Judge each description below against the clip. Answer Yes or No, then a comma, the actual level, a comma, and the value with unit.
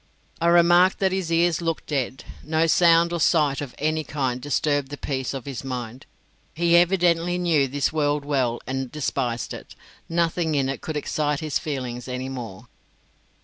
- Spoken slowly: No, average, 170 wpm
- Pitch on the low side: No, medium, 150 Hz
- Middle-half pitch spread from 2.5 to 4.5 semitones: Yes, average, 4.0 semitones